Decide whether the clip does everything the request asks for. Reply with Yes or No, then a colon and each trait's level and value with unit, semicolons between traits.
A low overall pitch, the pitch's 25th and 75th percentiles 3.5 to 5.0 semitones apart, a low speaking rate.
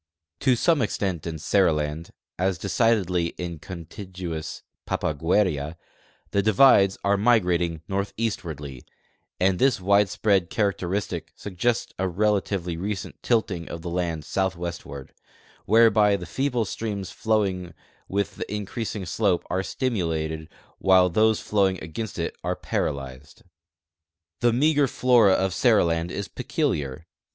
Yes: very low, 95 Hz; average, 4.0 semitones; slow, 120 wpm